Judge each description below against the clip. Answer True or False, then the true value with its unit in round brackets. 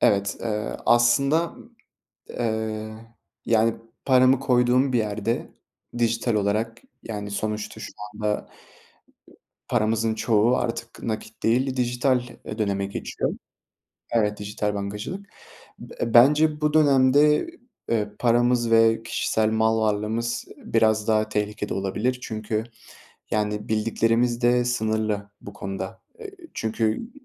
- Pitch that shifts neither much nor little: False (2.3 semitones)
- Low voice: True (110 Hz)